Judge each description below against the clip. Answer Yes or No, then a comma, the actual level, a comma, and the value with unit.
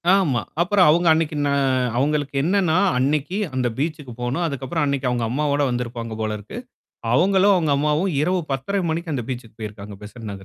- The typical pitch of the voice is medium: Yes, medium, 145 Hz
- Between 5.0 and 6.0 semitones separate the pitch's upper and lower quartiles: Yes, wide, 5.4 semitones